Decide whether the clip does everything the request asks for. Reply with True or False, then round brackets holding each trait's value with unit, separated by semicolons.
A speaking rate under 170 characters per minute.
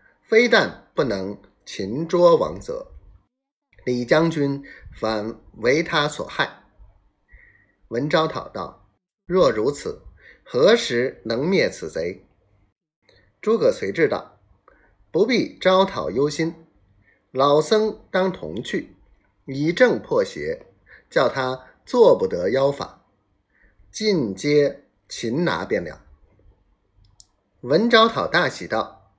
True (140 characters per minute)